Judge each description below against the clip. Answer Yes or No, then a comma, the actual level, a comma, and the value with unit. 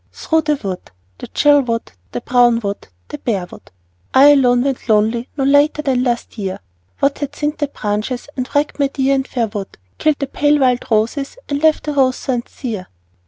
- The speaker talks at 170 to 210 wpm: Yes, average, 200 wpm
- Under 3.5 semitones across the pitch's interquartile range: No, average, 3.8 semitones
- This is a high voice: Yes, very high, 260 Hz